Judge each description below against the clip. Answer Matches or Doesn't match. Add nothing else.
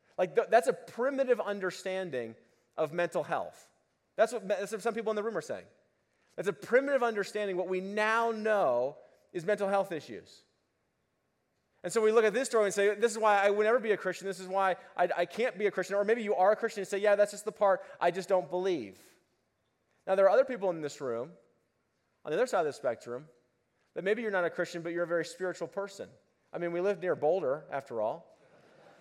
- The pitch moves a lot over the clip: Doesn't match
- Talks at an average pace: Doesn't match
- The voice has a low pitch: Doesn't match